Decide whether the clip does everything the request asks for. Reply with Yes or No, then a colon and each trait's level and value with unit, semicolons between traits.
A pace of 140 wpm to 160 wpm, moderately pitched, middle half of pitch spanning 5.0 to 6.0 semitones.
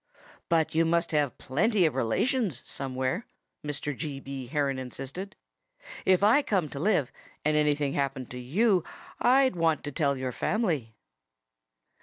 Yes: average, 150 wpm; medium, 150 Hz; average, 5.3 semitones